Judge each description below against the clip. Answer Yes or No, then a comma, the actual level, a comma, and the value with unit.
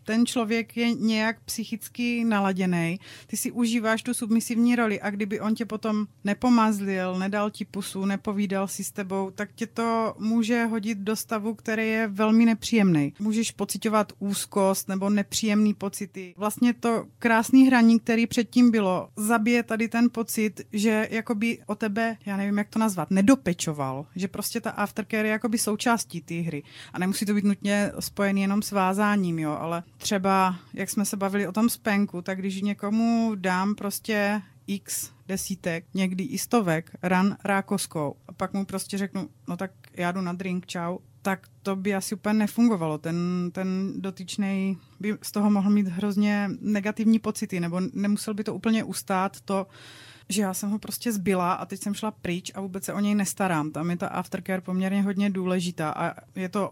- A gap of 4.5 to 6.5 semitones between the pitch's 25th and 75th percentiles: No, narrow, 2.5 semitones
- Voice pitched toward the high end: Yes, high, 205 Hz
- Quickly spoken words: Yes, fast, 175 wpm